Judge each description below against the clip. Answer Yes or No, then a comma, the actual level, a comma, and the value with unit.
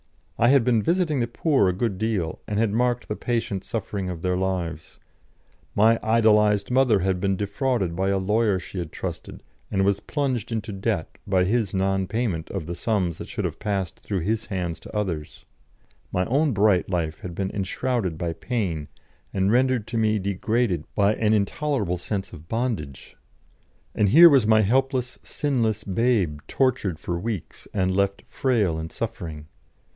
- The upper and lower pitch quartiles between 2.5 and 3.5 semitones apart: No, average, 4.0 semitones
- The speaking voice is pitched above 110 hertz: No, low, 100 Hz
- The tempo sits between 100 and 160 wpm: No, average, 170 wpm